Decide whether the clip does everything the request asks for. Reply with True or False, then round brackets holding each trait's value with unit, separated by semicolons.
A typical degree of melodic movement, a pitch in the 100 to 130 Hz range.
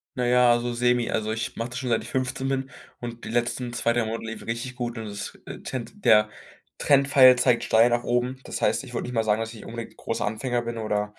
False (1.8 semitones; 120 Hz)